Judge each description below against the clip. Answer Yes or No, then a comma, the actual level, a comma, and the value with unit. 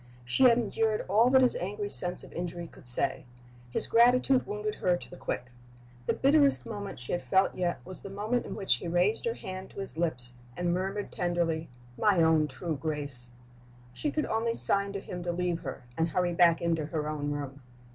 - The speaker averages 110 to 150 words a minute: No, fast, 205 wpm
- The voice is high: No, medium, 180 Hz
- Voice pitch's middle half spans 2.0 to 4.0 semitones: No, average, 4.5 semitones